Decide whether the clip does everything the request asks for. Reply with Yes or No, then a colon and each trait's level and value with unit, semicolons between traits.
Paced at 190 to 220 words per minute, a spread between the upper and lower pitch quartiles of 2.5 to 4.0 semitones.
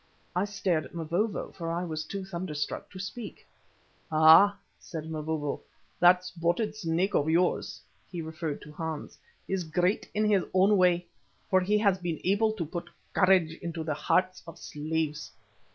No: average, 165 wpm; average, 3.1 semitones